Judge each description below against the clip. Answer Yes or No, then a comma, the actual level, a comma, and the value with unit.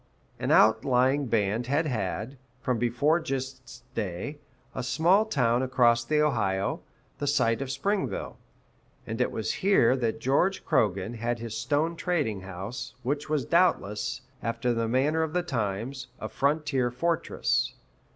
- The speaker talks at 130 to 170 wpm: Yes, average, 140 wpm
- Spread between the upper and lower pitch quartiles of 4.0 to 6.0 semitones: Yes, average, 4.7 semitones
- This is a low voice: Yes, low, 125 Hz